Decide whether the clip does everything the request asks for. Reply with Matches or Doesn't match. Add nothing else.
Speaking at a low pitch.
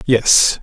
Matches